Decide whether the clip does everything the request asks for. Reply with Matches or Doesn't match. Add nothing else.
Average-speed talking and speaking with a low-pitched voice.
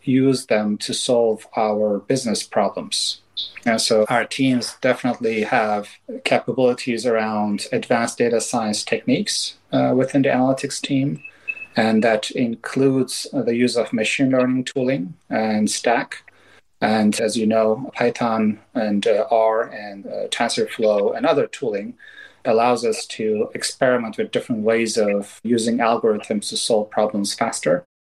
Matches